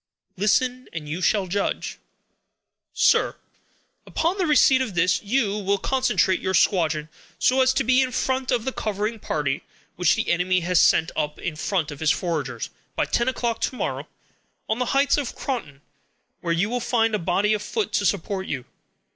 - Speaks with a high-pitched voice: Yes, high, 205 Hz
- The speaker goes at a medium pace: Yes, average, 180 wpm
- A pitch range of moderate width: No, wide, 6.6 semitones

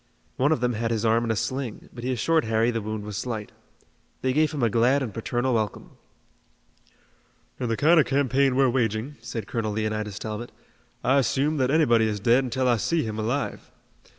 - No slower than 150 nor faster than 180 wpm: No, average, 200 wpm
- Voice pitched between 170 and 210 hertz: No, low, 120 Hz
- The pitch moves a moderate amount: Yes, average, 3.4 semitones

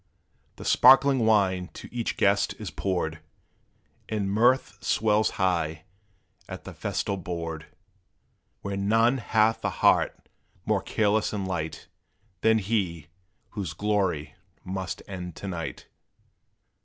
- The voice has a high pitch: No, low, 100 Hz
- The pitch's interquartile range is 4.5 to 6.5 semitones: No, average, 3.7 semitones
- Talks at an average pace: No, slow, 120 wpm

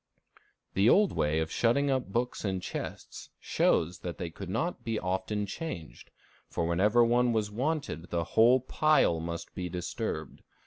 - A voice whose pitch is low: Yes, low, 105 Hz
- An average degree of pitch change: No, wide, 6.3 semitones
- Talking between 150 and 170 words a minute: Yes, average, 160 wpm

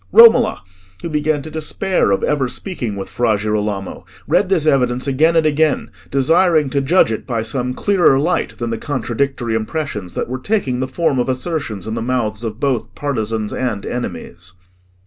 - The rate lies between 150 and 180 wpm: Yes, average, 175 wpm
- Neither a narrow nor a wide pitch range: No, wide, 5.7 semitones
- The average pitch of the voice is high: No, low, 130 Hz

